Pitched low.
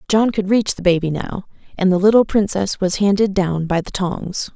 No: high, 190 Hz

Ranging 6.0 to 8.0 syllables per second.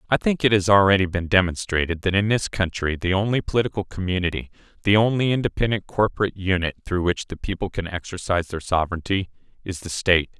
Yes: 6.4 syllables/s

